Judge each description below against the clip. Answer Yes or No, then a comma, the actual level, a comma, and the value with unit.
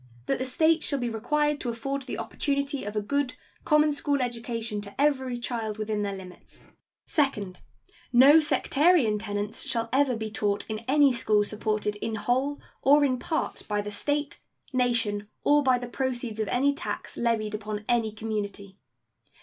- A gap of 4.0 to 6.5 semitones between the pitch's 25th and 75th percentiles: Yes, average, 4.8 semitones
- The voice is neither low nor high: No, high, 240 Hz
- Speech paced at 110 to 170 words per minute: Yes, average, 165 wpm